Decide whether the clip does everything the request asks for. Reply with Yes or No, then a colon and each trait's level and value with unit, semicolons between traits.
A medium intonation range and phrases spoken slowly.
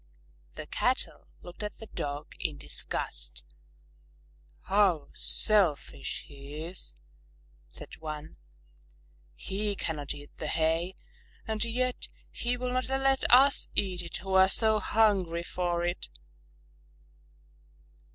No: wide, 5.8 semitones; slow, 110 wpm